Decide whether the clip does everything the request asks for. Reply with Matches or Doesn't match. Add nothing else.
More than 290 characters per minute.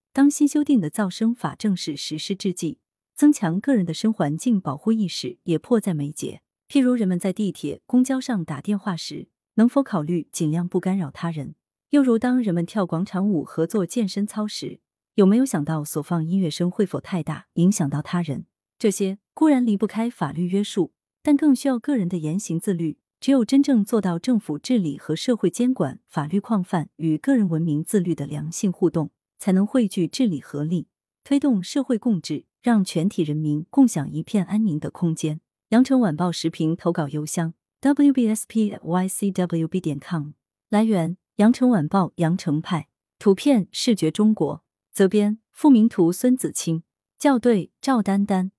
Doesn't match